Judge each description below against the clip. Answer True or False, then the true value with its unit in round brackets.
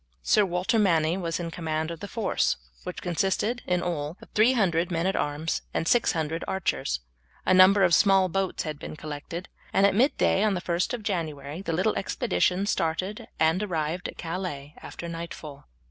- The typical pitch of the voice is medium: True (175 Hz)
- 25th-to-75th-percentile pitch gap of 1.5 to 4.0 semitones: True (3.3 semitones)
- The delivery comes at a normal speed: True (175 wpm)